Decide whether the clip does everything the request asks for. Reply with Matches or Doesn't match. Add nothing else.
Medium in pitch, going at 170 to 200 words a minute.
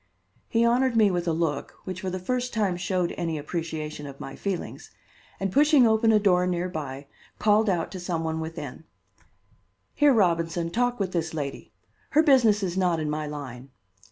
Matches